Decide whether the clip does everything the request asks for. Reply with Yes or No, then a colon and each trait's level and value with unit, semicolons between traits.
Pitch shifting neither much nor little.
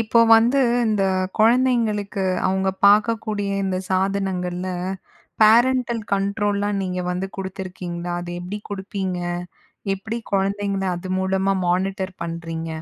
No: narrow, 2.2 semitones